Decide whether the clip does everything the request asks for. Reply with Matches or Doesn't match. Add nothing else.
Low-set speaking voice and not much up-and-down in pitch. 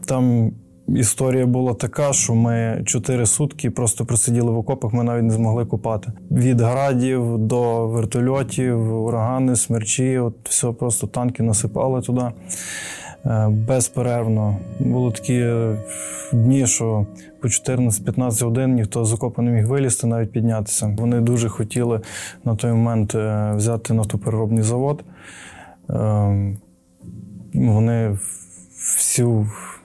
Matches